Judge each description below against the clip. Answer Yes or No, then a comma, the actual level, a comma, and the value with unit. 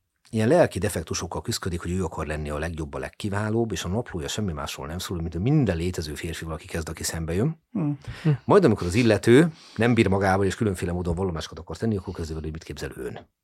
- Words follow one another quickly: Yes, fast, 215 wpm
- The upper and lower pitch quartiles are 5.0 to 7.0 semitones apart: Yes, wide, 5.4 semitones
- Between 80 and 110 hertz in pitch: Yes, very low, 95 Hz